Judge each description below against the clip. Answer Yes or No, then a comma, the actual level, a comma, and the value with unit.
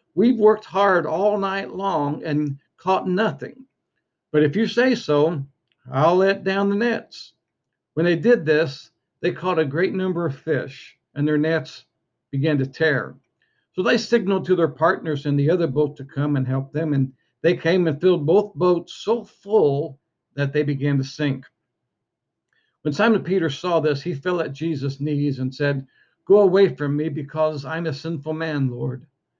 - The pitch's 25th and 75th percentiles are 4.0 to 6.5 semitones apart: Yes, average, 4.4 semitones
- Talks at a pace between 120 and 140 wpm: No, average, 180 wpm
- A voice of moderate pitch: Yes, medium, 160 Hz